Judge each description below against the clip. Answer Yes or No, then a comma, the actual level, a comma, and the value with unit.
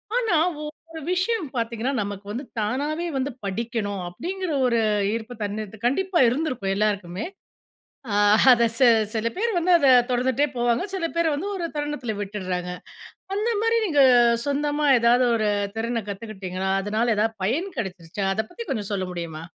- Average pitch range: No, wide, 7.0 semitones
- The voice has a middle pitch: No, high, 235 Hz